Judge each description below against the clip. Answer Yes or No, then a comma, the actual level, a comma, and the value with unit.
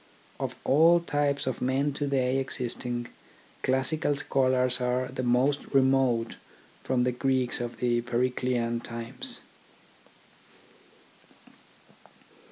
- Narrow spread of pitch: Yes, narrow, 1.8 semitones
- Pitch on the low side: Yes, low, 130 Hz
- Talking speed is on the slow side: Yes, slow, 100 wpm